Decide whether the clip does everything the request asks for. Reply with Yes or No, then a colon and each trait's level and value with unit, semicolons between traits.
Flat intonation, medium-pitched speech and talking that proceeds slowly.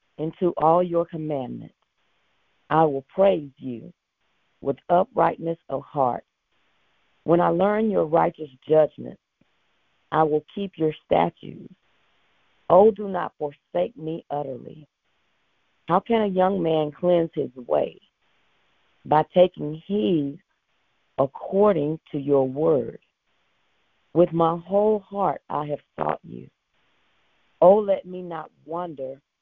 No: average, 3.4 semitones; medium, 165 Hz; slow, 115 wpm